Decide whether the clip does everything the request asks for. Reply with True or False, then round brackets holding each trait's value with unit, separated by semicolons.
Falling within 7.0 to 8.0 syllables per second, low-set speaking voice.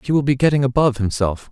True (7.1 syllables/s; 130 Hz)